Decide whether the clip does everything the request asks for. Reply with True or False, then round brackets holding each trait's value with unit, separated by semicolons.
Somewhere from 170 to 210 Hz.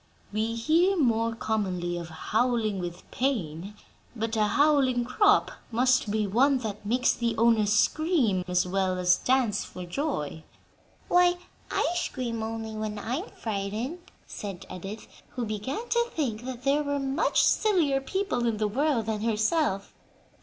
False (230 Hz)